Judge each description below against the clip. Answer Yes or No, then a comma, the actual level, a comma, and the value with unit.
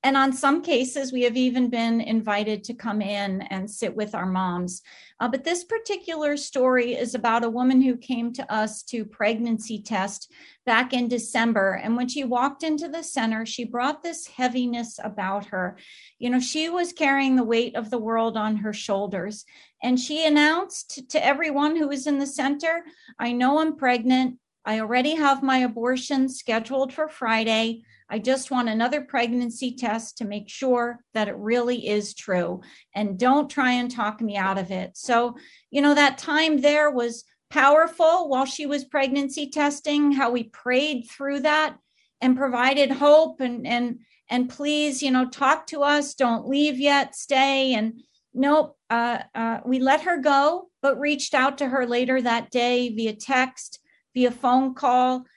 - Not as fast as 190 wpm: Yes, average, 175 wpm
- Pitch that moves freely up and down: No, average, 3.7 semitones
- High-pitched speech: Yes, very high, 255 Hz